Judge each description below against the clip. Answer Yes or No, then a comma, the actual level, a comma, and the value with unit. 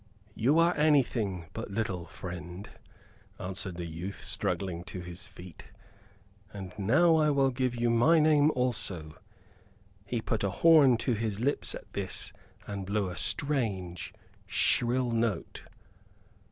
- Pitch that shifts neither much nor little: No, wide, 5.8 semitones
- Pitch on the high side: No, low, 110 Hz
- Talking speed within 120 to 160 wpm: Yes, slow, 135 wpm